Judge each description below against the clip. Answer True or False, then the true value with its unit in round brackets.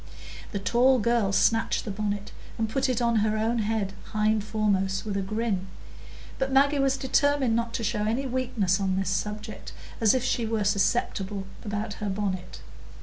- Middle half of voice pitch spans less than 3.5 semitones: True (2.8 semitones)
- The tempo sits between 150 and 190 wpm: True (175 wpm)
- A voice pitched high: True (215 Hz)